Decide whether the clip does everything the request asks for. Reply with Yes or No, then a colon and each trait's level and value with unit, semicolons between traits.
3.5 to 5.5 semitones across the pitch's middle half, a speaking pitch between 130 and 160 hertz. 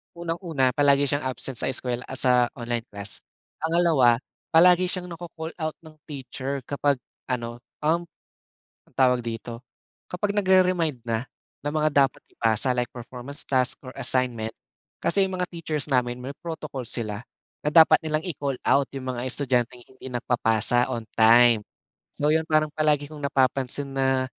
Yes: average, 4.2 semitones; low, 135 Hz